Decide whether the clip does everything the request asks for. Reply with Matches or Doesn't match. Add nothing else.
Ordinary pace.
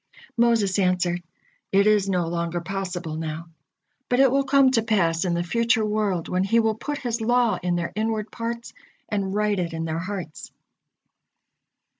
Matches